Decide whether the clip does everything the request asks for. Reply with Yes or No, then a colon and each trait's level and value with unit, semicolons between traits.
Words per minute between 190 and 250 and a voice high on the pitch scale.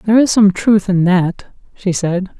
Yes: average, 200 wpm; high, 195 Hz